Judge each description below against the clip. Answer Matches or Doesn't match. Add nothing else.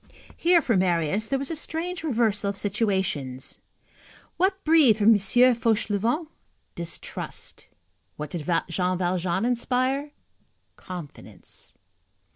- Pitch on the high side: Matches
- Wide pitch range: Matches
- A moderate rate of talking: Doesn't match